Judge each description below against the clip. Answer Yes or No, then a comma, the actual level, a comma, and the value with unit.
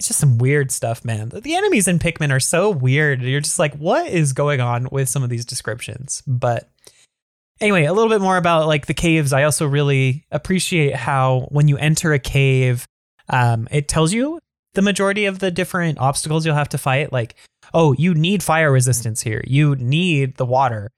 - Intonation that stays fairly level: No, average, 4.2 semitones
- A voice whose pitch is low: No, medium, 145 Hz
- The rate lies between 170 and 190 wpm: No, average, 200 wpm